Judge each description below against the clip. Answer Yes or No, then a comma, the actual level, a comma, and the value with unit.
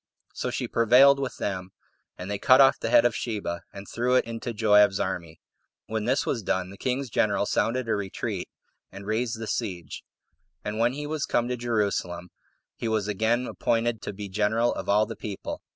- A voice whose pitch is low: Yes, low, 110 Hz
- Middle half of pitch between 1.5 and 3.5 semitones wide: Yes, average, 3.2 semitones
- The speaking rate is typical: Yes, average, 195 wpm